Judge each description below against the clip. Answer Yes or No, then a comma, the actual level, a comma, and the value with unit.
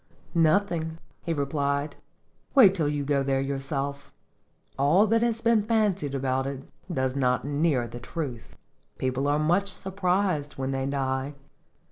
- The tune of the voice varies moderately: Yes, average, 4.9 semitones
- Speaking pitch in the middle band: Yes, medium, 145 Hz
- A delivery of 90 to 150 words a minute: Yes, average, 140 wpm